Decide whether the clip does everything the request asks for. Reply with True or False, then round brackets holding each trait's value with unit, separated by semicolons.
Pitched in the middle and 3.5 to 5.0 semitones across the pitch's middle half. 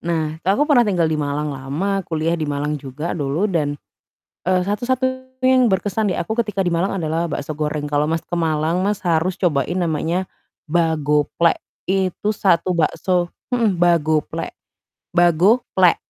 True (170 Hz; 3.9 semitones)